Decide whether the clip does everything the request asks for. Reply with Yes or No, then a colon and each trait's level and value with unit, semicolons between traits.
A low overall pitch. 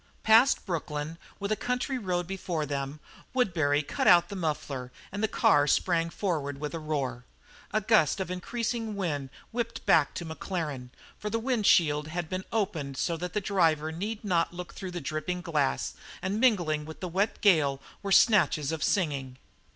No: medium, 175 Hz